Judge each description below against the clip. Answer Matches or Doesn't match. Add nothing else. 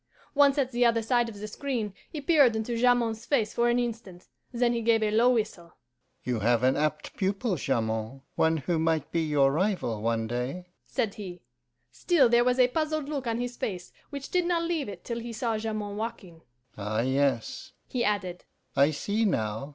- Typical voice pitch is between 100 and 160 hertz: Doesn't match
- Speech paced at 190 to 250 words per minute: Matches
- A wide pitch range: Matches